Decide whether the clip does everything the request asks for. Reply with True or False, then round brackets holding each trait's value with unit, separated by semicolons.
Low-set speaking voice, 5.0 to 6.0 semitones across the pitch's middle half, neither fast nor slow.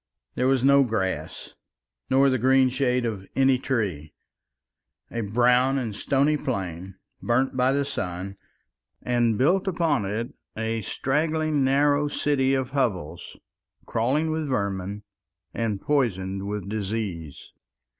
False (125 Hz; 5.3 semitones; 125 wpm)